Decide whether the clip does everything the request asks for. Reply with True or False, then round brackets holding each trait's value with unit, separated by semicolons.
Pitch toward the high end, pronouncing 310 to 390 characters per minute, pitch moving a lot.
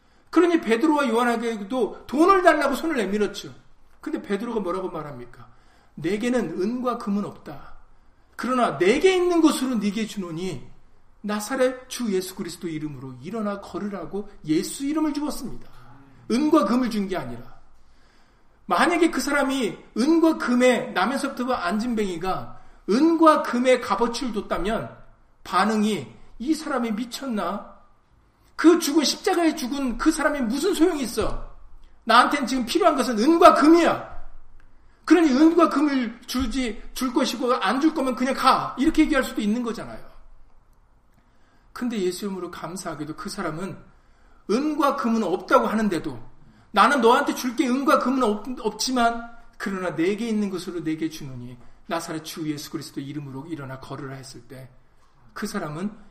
True (235 Hz; 315 characters per minute; 6.9 semitones)